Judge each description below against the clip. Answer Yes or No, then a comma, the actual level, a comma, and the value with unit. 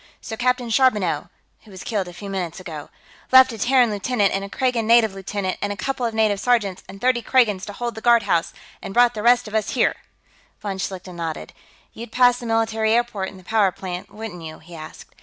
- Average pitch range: Yes, average, 3.9 semitones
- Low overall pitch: No, high, 215 Hz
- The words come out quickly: Yes, fast, 215 wpm